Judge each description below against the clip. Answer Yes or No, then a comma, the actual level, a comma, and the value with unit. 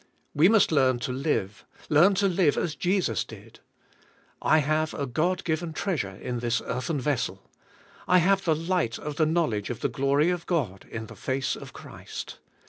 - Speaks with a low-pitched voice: No, medium, 150 Hz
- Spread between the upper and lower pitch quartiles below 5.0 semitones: No, wide, 5.5 semitones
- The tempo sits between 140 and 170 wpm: No, average, 180 wpm